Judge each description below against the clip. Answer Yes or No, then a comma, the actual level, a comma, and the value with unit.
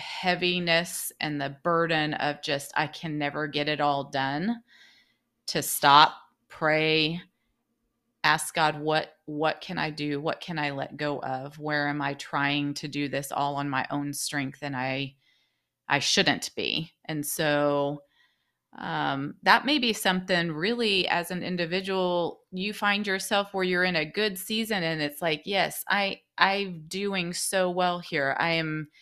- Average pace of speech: Yes, average, 160 wpm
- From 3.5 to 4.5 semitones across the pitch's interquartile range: Yes, average, 4.2 semitones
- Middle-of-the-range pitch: Yes, medium, 155 Hz